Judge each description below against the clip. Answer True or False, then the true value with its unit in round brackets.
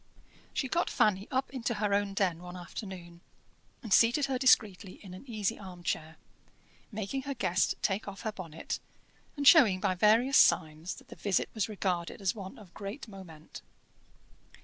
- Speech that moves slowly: False (170 wpm)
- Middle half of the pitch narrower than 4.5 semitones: True (4.0 semitones)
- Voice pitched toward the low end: False (200 Hz)